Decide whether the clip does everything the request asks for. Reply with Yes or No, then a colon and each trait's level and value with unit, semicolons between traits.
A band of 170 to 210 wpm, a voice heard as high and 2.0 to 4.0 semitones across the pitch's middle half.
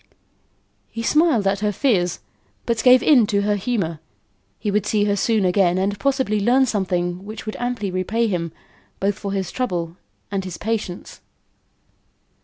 No: average, 160 wpm; high, 205 Hz; average, 3.6 semitones